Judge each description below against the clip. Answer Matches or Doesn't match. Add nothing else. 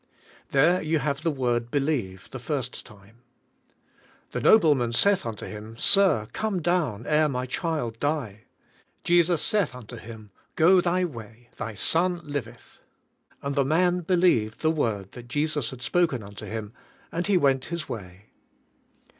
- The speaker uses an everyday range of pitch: Doesn't match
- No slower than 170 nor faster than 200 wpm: Doesn't match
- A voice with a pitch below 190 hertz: Matches